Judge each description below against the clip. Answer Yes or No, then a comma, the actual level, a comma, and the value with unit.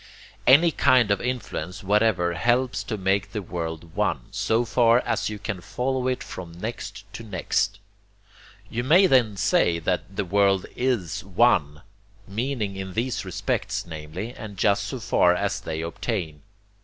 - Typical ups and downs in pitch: Yes, average, 5.0 semitones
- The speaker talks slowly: No, average, 155 wpm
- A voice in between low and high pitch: No, low, 100 Hz